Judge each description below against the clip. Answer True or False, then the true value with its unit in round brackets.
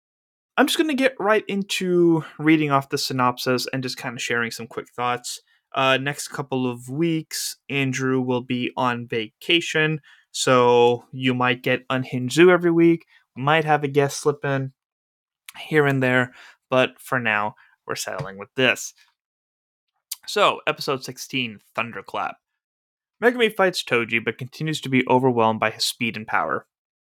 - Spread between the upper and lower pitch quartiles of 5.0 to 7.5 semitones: False (4.0 semitones)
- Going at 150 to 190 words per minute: True (155 wpm)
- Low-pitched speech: True (130 Hz)